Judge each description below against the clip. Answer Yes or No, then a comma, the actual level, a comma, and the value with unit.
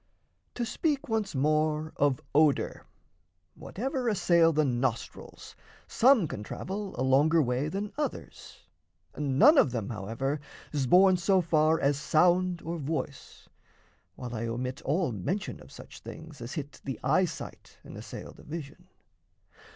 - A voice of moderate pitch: Yes, medium, 155 Hz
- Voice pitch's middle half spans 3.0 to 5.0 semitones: No, wide, 5.5 semitones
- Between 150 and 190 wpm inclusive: No, average, 140 wpm